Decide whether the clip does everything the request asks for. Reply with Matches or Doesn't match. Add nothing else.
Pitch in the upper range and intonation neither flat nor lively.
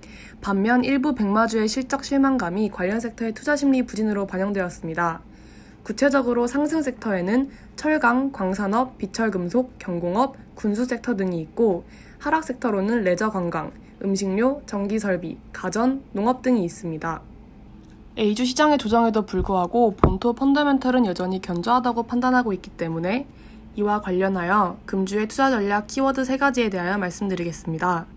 Matches